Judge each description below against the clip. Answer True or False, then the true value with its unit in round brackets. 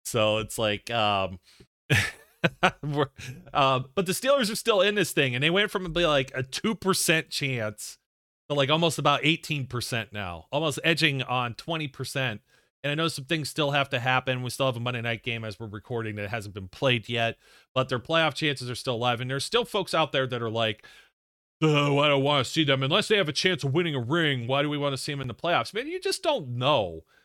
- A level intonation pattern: False (4.9 semitones)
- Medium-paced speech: False (230 wpm)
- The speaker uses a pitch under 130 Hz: False (135 Hz)